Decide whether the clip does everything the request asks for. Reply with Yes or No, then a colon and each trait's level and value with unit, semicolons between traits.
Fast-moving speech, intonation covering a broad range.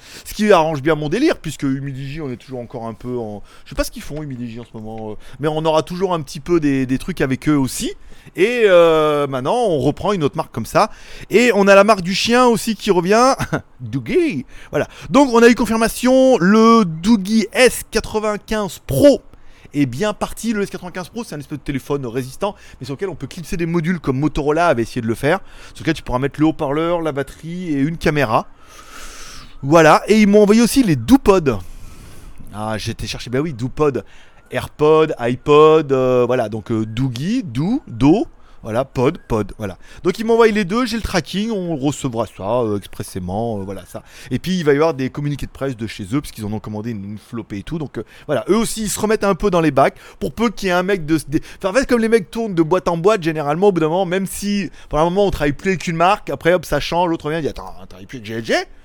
Yes: fast, 240 wpm; wide, 7.8 semitones